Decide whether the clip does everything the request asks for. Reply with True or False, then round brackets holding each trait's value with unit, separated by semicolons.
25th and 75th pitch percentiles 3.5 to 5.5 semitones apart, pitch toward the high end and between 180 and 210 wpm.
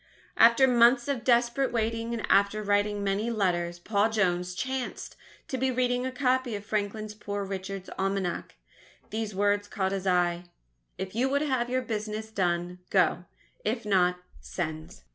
False (3.8 semitones; 210 Hz; 155 wpm)